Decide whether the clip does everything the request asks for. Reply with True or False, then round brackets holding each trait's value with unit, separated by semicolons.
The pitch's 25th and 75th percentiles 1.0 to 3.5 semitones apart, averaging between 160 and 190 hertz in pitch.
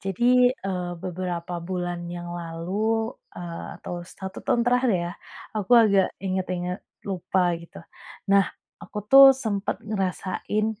True (3.2 semitones; 185 Hz)